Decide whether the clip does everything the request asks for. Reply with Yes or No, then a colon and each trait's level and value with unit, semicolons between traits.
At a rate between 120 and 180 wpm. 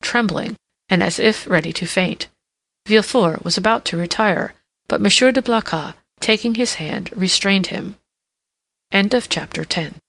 Yes: slow, 135 wpm